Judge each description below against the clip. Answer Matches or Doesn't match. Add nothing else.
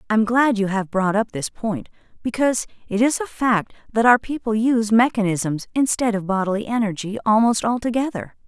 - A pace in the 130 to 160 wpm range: Doesn't match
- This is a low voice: Doesn't match